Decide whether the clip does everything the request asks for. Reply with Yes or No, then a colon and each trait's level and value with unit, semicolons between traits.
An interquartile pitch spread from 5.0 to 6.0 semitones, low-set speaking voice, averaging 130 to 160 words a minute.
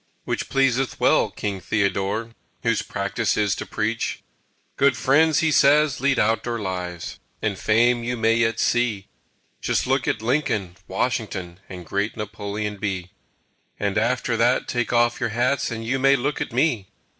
No: average, 3.6 semitones; low, 115 Hz; average, 155 wpm